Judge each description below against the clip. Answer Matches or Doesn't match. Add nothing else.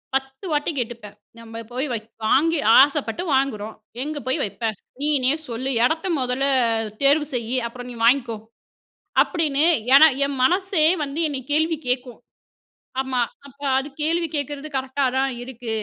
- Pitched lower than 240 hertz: Doesn't match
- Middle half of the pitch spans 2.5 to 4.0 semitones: Matches